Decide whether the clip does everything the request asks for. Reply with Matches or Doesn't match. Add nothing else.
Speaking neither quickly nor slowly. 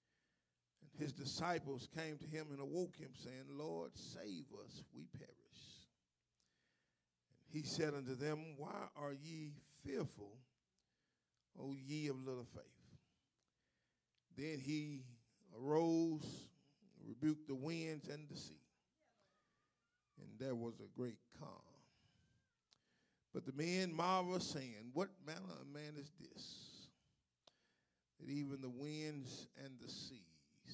Doesn't match